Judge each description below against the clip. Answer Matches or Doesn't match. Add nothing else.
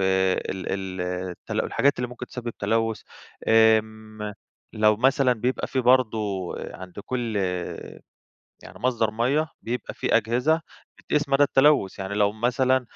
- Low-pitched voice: Matches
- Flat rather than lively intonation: Doesn't match